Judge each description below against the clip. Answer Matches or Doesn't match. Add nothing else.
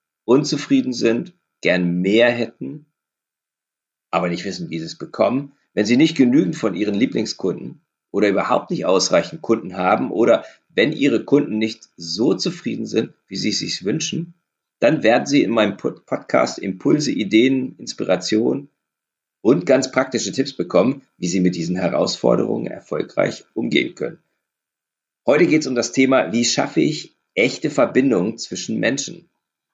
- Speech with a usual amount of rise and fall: Doesn't match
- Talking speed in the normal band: Matches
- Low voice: Matches